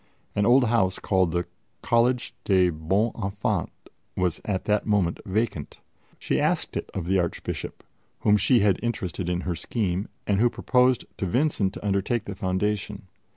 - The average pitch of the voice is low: Yes, low, 100 Hz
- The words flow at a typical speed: Yes, average, 160 wpm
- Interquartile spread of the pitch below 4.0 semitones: Yes, average, 3.5 semitones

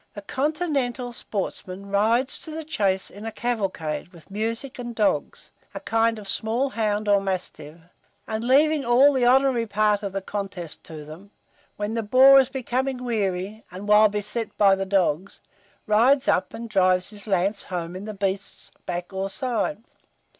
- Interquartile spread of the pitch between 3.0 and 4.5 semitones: Yes, average, 3.9 semitones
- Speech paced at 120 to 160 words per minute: No, average, 170 wpm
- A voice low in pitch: No, high, 210 Hz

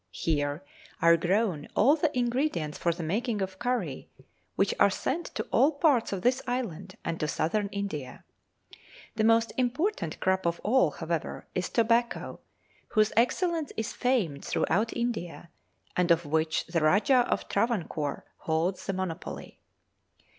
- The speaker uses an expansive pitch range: Yes, wide, 6.4 semitones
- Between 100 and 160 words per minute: Yes, average, 145 wpm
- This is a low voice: No, high, 200 Hz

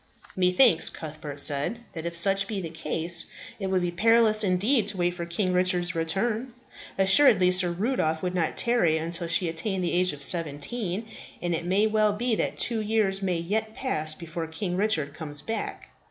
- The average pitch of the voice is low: No, medium, 180 Hz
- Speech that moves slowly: No, average, 185 wpm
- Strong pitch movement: No, average, 4.2 semitones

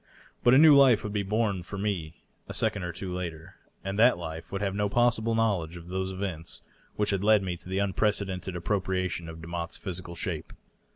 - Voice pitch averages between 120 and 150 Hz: No, very low, 95 Hz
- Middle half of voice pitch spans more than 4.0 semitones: No, average, 3.2 semitones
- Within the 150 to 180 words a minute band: No, fast, 205 wpm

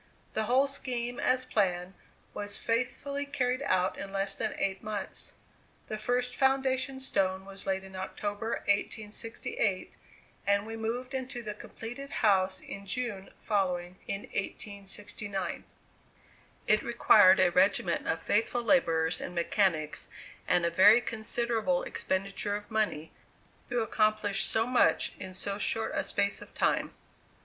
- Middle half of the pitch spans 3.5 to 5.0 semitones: Yes, average, 3.8 semitones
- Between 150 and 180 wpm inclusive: No, slow, 135 wpm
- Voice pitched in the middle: No, high, 210 Hz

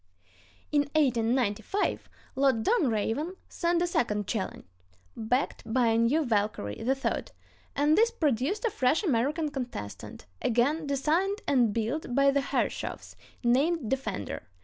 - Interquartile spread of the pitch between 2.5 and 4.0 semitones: No, average, 5.3 semitones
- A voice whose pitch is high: Yes, very high, 270 Hz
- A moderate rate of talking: No, slow, 125 wpm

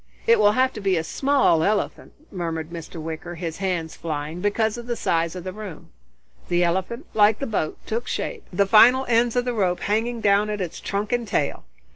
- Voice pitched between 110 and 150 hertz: No, high, 200 Hz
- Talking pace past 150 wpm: Yes, fast, 205 wpm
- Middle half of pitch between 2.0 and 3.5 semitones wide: No, average, 5.2 semitones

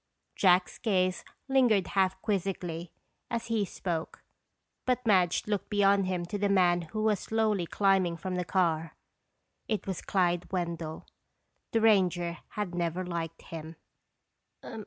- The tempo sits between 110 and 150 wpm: Yes, slow, 135 wpm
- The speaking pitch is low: No, medium, 185 Hz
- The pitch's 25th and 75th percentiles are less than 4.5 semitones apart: Yes, average, 3.0 semitones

